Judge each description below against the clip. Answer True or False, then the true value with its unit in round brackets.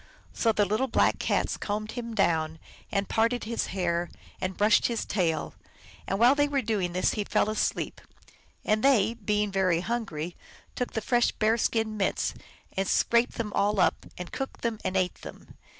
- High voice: True (210 Hz)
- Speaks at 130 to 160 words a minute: False (175 wpm)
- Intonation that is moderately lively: True (3.5 semitones)